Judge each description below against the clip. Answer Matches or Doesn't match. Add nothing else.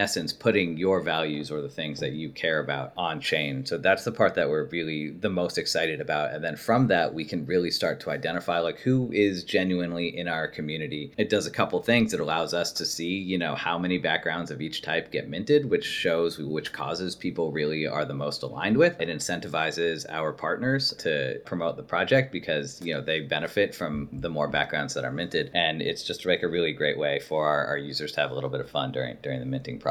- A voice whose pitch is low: Matches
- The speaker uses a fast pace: Matches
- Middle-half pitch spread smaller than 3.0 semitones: Doesn't match